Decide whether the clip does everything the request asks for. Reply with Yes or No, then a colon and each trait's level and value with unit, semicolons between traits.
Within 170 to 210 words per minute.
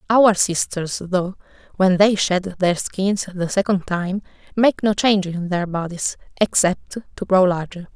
No: average, 160 wpm